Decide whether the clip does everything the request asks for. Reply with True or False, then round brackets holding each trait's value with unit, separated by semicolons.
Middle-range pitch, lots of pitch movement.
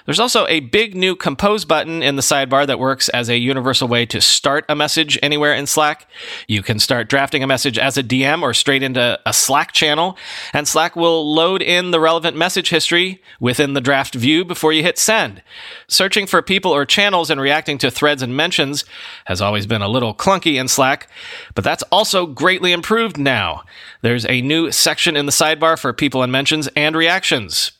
False (150 Hz; 4.3 semitones)